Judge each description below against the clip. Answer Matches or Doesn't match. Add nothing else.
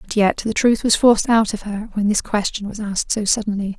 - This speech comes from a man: Doesn't match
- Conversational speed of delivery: Doesn't match